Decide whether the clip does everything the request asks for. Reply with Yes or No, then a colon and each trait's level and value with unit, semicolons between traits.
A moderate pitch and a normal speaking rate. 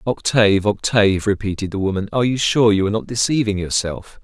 No: low, 105 Hz; average, 185 wpm